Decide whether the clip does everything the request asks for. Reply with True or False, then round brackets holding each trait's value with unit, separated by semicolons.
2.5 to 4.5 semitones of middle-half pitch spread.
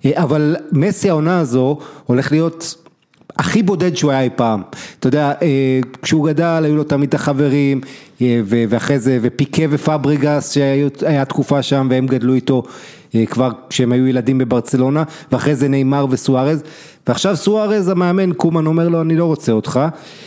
True (3.7 semitones)